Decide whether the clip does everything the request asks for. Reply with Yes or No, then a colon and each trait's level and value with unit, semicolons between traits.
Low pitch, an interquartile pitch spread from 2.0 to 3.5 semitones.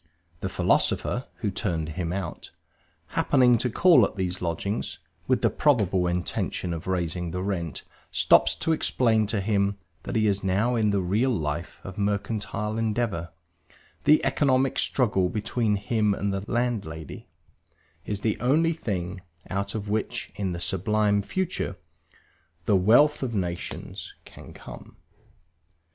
No: low, 100 Hz; average, 3.9 semitones